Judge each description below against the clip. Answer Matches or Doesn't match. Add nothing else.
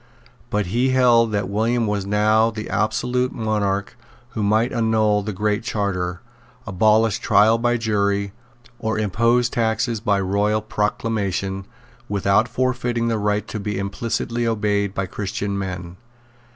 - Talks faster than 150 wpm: Doesn't match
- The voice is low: Matches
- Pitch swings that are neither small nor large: Doesn't match